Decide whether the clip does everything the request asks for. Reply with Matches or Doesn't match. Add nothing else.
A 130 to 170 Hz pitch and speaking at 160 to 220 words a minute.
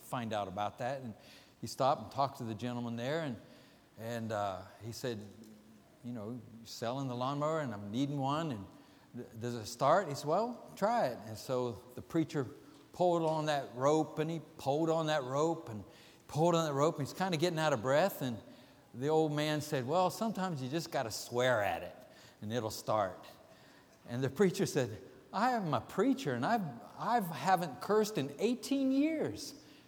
Matches